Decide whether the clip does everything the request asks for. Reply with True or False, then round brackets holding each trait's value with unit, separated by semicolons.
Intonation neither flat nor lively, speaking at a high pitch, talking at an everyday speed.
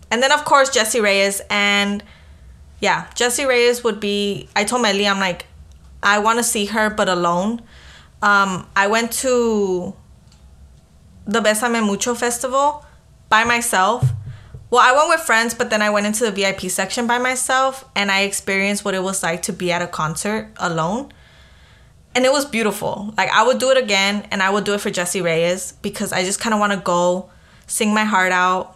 True (4.2 semitones; 205 Hz; 190 wpm)